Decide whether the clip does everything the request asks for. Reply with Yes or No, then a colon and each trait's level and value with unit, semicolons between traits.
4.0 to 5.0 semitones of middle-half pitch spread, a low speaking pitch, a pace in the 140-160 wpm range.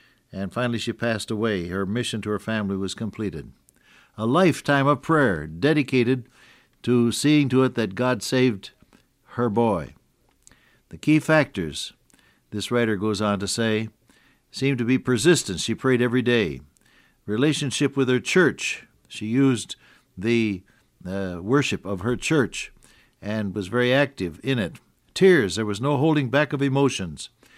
Yes: average, 4.4 semitones; low, 120 Hz; average, 150 wpm